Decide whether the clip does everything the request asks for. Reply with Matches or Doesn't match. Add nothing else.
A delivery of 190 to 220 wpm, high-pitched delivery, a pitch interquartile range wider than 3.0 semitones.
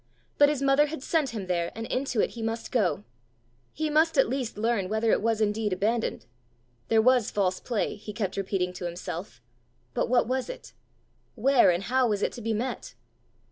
Matches